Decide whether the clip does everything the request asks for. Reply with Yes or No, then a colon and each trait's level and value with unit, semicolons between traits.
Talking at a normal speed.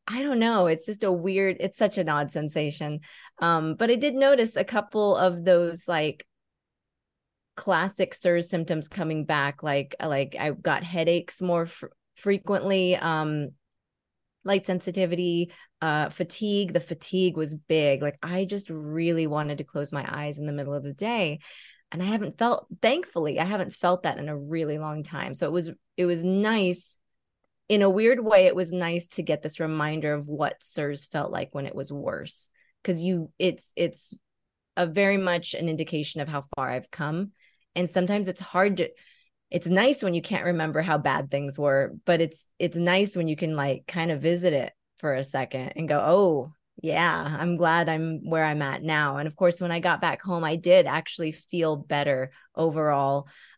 Yes: average, 190 wpm